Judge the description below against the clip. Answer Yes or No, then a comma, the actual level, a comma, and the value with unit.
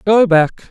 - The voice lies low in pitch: No, high, 190 Hz